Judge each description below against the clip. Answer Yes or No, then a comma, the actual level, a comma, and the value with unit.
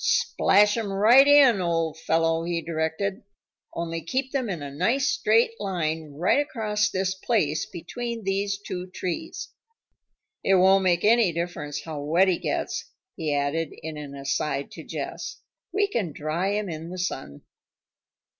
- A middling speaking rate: Yes, average, 155 wpm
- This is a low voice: No, medium, 180 Hz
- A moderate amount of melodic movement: Yes, average, 4.7 semitones